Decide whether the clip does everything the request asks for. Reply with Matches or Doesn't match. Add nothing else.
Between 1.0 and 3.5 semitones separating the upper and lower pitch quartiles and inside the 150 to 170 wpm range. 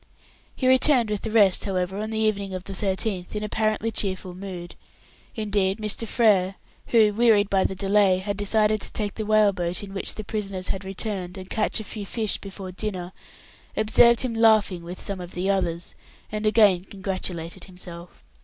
Doesn't match